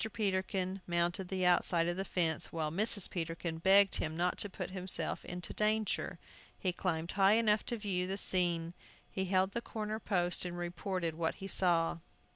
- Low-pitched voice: No, medium, 185 Hz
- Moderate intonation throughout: No, narrow, 2.2 semitones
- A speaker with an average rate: Yes, average, 180 wpm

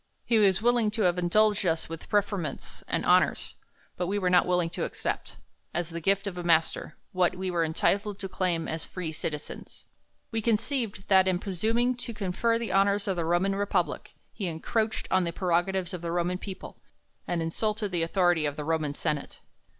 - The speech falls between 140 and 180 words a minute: No, average, 195 wpm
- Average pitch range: Yes, average, 3.3 semitones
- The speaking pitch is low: No, medium, 185 Hz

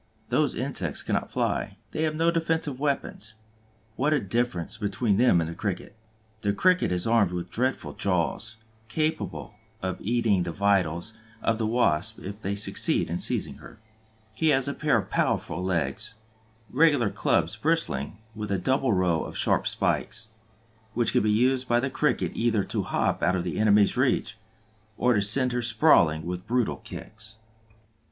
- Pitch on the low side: Yes, low, 110 Hz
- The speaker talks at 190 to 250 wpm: No, average, 170 wpm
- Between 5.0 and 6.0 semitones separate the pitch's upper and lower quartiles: Yes, average, 5.3 semitones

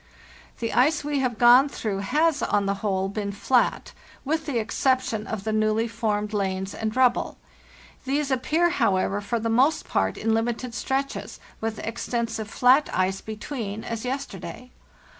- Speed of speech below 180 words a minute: Yes, average, 160 wpm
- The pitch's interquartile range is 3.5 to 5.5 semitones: Yes, average, 3.9 semitones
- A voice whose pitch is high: Yes, high, 230 Hz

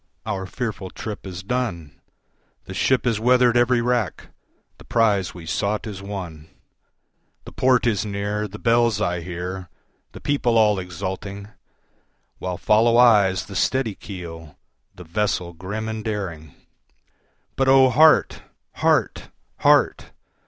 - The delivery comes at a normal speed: No, slow, 130 wpm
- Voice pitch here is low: Yes, low, 105 Hz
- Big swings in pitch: No, average, 4.2 semitones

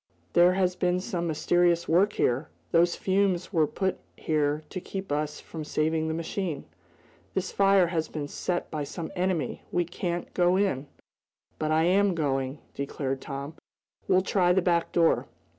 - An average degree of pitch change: Yes, average, 3.1 semitones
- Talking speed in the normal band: Yes, average, 160 wpm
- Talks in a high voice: No, medium, 170 Hz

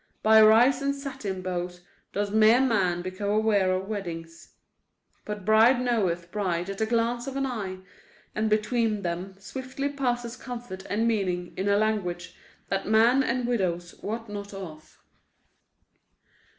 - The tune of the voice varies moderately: Yes, average, 4.2 semitones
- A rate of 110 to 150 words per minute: Yes, average, 145 wpm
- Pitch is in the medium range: No, high, 210 Hz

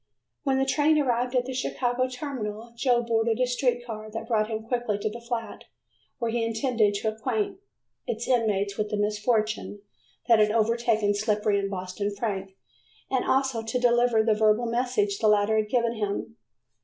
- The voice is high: Yes, high, 225 Hz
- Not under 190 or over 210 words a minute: No, average, 175 wpm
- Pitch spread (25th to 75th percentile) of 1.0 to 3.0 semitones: Yes, narrow, 2.6 semitones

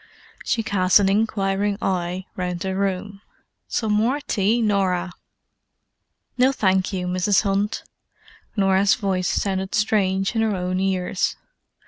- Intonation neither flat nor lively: No, narrow, 2.0 semitones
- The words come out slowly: Yes, slow, 125 wpm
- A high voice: Yes, high, 195 Hz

